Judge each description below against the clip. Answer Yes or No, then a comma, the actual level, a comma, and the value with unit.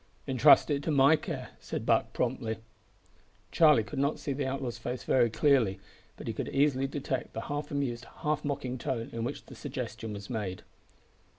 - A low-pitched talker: Yes, low, 130 Hz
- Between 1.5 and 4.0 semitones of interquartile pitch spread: Yes, average, 3.7 semitones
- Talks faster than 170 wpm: Yes, average, 180 wpm